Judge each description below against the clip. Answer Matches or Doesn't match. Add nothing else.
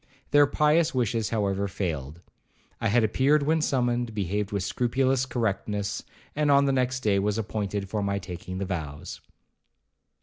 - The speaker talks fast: Doesn't match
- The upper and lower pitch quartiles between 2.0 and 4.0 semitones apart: Doesn't match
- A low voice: Matches